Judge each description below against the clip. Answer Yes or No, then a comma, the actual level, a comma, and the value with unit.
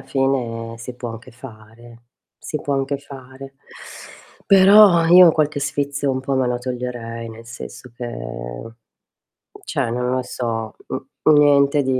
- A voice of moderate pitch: No, low, 130 Hz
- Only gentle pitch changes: No, average, 3.4 semitones